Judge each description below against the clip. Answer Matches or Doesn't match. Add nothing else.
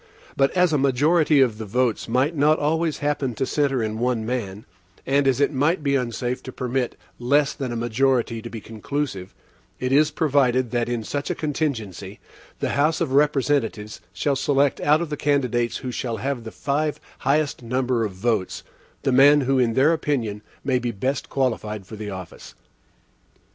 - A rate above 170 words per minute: Matches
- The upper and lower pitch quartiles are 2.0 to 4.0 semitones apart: Matches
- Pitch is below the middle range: Matches